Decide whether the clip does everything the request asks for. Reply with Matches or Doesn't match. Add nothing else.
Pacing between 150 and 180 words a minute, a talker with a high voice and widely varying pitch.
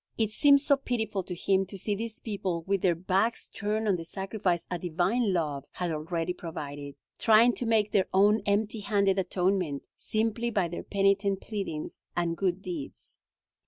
Doesn't match